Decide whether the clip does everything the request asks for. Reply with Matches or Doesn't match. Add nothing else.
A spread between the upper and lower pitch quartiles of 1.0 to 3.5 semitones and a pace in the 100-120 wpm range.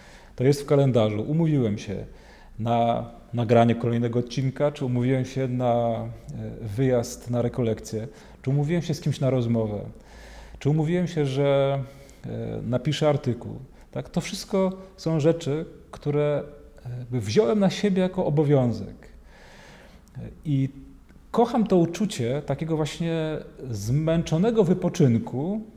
Doesn't match